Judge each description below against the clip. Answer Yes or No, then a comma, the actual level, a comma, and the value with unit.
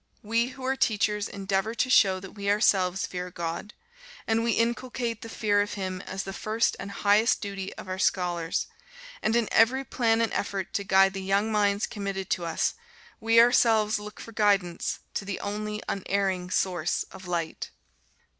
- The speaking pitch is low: No, high, 205 Hz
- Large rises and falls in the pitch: No, average, 2.7 semitones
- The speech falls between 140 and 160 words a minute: No, average, 175 wpm